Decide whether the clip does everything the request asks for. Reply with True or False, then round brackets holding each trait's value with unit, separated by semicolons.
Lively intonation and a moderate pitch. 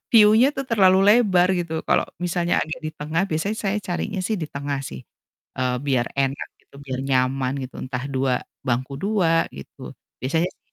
True (6.6 semitones; 160 Hz)